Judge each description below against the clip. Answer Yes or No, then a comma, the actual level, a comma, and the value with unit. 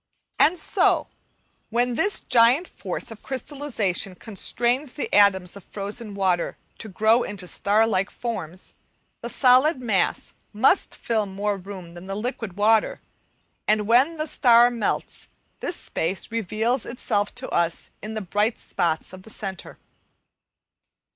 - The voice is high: Yes, high, 215 Hz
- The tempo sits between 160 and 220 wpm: No, average, 140 wpm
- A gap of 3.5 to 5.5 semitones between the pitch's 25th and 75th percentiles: Yes, average, 3.8 semitones